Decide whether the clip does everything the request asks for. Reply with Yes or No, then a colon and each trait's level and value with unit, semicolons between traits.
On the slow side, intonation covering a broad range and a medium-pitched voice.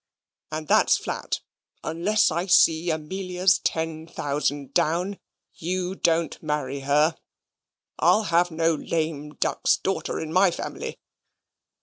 No: slow, 115 wpm; average, 2.9 semitones; medium, 165 Hz